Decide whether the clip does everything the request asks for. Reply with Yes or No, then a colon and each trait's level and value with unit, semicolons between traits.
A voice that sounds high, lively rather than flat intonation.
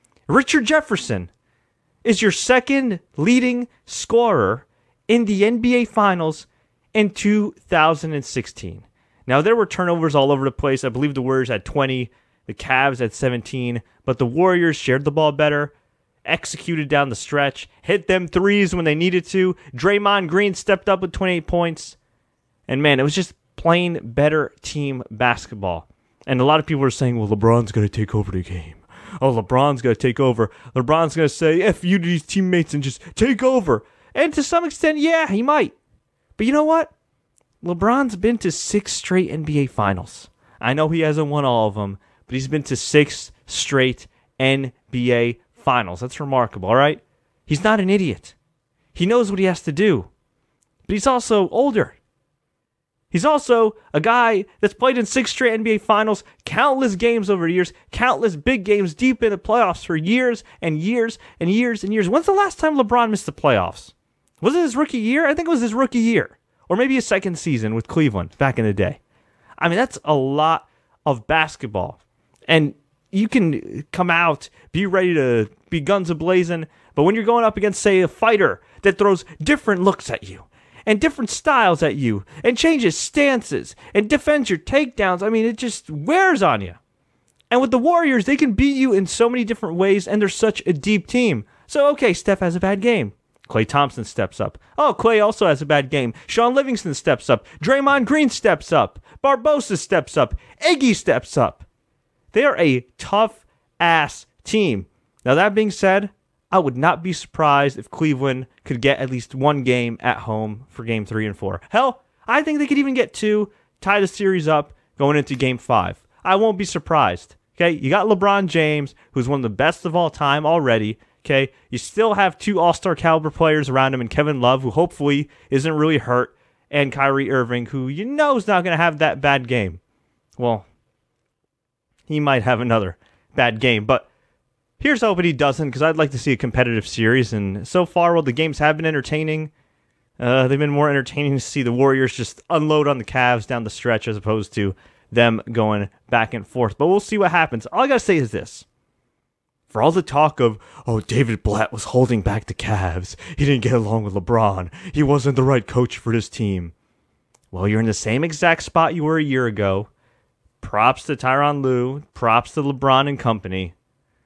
No: medium, 155 Hz; wide, 8.3 semitones